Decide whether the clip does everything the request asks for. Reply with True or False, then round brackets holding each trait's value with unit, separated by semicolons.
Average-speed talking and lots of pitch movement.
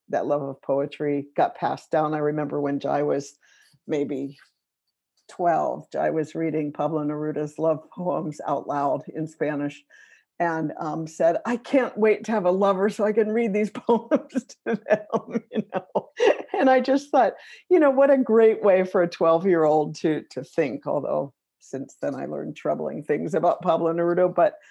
True (175 wpm; 7.1 semitones)